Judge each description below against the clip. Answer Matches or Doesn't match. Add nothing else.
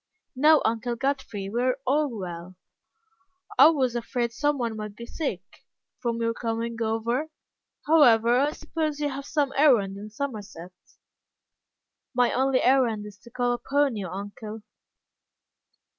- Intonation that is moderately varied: Matches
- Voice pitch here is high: Matches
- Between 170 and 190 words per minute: Doesn't match